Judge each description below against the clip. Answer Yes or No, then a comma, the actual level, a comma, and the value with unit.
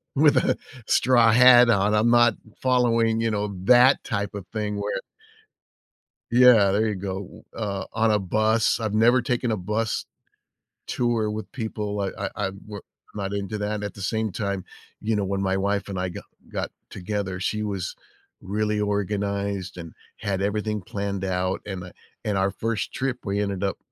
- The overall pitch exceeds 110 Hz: No, low, 105 Hz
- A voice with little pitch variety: Yes, narrow, 2.2 semitones